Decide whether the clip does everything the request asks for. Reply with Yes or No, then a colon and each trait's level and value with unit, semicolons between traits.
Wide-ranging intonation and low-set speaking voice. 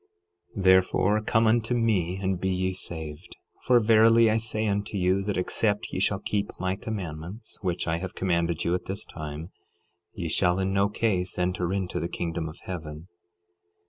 No: average, 3.4 semitones; very low, 95 Hz